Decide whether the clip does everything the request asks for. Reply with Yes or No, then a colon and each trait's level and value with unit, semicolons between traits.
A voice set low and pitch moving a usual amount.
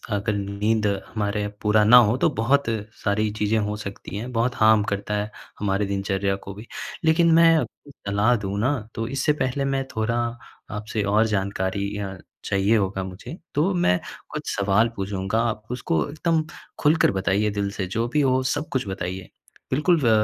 Yes: low, 105 Hz; average, 3.7 semitones